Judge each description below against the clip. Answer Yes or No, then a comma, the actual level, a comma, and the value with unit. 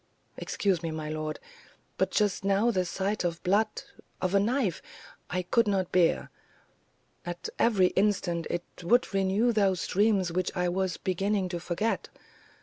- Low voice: No, high, 190 Hz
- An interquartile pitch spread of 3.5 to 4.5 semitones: No, average, 2.9 semitones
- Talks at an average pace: Yes, average, 150 wpm